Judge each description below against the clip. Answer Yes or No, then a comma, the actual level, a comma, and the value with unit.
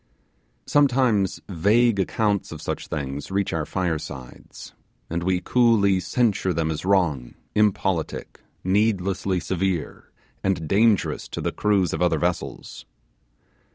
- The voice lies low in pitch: Yes, very low, 95 Hz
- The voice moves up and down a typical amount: Yes, average, 3.8 semitones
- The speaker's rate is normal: No, slow, 120 wpm